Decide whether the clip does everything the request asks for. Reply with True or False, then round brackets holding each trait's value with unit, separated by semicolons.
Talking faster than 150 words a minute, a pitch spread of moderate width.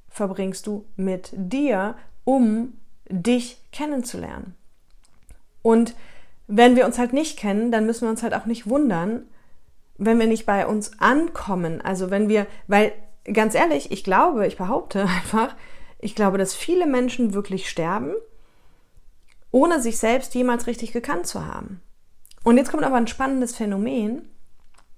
False (145 wpm; 3.4 semitones)